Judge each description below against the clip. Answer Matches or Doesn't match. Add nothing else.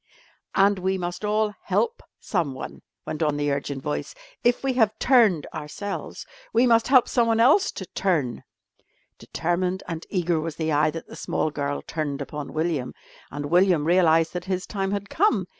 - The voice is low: Doesn't match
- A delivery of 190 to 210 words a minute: Doesn't match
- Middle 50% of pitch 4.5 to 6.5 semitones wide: Matches